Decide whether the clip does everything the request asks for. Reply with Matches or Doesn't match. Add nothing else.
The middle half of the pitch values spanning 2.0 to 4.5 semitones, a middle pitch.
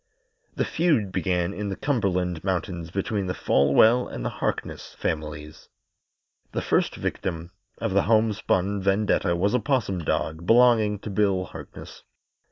Doesn't match